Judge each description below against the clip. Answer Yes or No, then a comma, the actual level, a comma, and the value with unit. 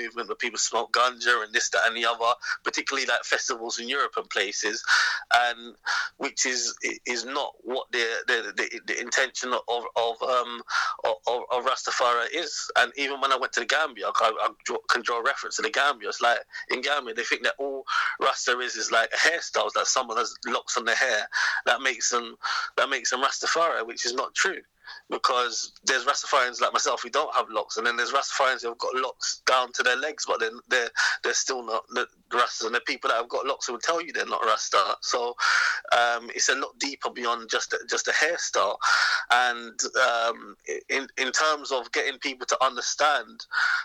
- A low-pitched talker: Yes, low, 130 Hz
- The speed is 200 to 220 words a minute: Yes, fast, 205 wpm